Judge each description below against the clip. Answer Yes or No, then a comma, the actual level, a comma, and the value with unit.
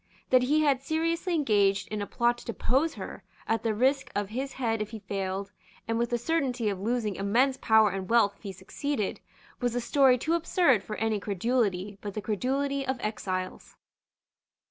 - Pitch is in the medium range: No, high, 230 Hz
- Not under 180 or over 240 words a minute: Yes, average, 190 wpm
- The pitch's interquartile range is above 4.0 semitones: Yes, average, 4.6 semitones